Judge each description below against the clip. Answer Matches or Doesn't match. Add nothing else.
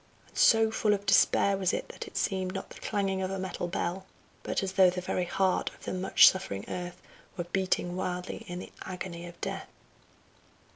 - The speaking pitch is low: Doesn't match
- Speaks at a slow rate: Doesn't match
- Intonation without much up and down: Matches